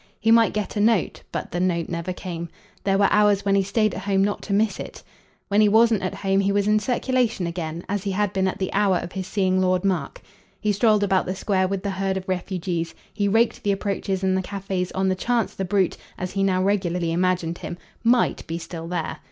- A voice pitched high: Yes, high, 195 Hz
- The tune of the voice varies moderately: No, narrow, 1.9 semitones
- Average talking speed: No, fast, 235 wpm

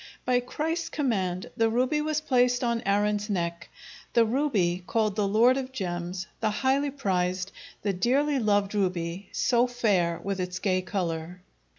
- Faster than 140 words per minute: Yes, average, 155 wpm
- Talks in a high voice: Yes, high, 210 Hz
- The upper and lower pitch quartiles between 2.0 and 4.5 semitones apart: No, average, 5.3 semitones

